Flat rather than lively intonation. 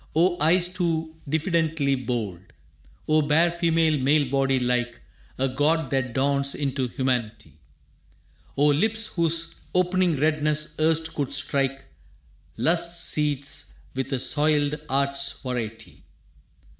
No: average, 3.3 semitones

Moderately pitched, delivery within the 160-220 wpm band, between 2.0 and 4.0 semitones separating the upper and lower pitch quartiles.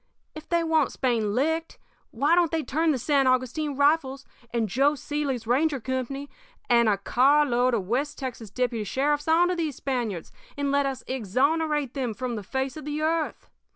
No: very high, 275 Hz; average, 180 wpm; average, 3.4 semitones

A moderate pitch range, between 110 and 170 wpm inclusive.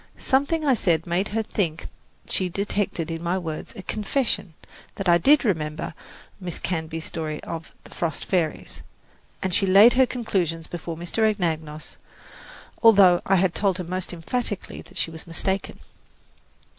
Yes: average, 3.9 semitones; average, 155 wpm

